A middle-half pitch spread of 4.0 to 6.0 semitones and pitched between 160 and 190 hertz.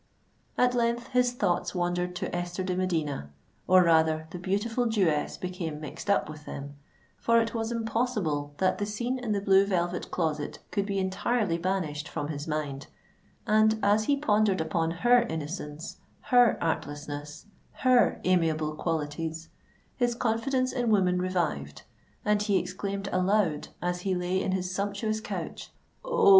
Yes: average, 5.2 semitones; medium, 185 Hz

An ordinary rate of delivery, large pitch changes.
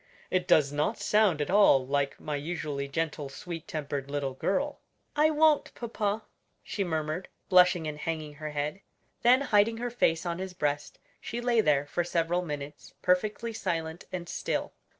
Yes: average, 165 wpm; wide, 5.8 semitones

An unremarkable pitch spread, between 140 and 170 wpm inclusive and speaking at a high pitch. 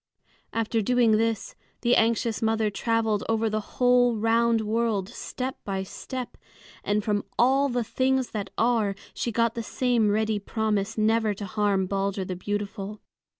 No: narrow, 2.2 semitones; average, 150 wpm; high, 220 Hz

